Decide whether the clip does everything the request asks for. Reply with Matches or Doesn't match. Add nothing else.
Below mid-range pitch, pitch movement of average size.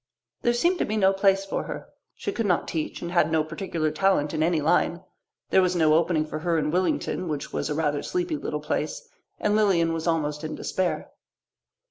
Doesn't match